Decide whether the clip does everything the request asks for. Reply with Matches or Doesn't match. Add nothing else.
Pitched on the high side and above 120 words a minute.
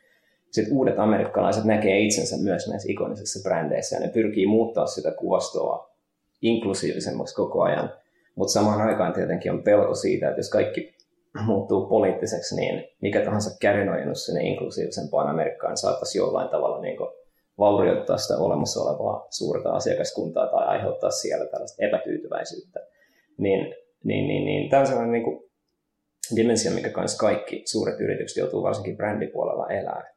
Matches